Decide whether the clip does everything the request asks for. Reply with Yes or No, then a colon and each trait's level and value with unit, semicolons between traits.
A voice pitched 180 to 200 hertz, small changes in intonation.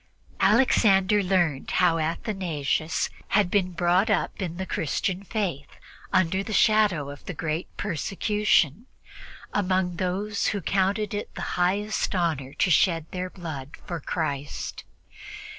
No: medium, 185 Hz; average, 3.6 semitones